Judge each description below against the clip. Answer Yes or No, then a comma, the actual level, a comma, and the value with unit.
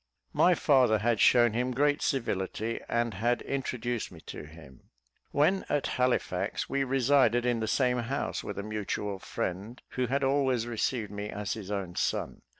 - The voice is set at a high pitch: No, low, 120 Hz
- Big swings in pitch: No, average, 3.9 semitones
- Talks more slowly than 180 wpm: Yes, average, 165 wpm